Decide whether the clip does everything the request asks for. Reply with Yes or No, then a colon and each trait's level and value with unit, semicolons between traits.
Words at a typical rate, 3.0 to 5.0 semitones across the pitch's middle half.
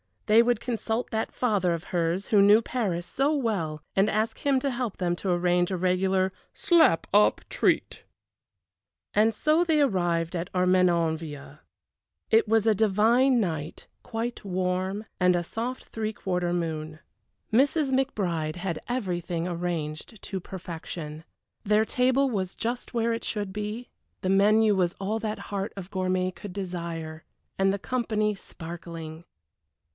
Yes: average, 145 wpm; average, 4.4 semitones